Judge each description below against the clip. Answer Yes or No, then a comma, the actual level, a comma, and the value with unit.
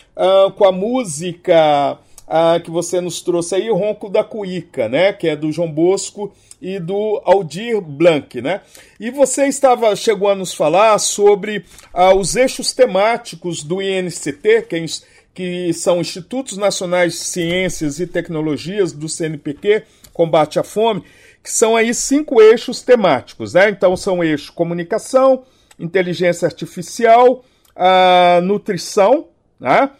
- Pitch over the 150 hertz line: Yes, high, 190 Hz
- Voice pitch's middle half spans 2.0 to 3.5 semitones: No, average, 4.0 semitones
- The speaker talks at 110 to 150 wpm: Yes, average, 140 wpm